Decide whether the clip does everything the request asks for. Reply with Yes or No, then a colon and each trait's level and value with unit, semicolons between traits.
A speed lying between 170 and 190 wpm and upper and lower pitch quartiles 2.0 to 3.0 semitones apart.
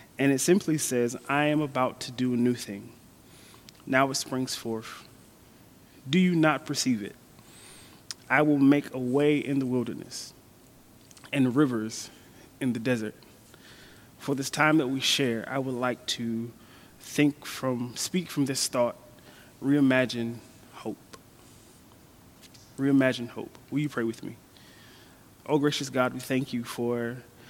No: average, 145 wpm; narrow, 2.6 semitones